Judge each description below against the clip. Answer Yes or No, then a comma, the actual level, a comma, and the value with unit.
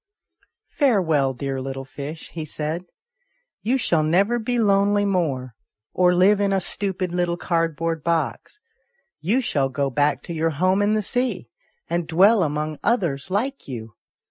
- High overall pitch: No, medium, 175 Hz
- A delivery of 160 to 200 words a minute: Yes, average, 165 wpm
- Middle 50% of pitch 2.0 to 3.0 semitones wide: No, average, 5.2 semitones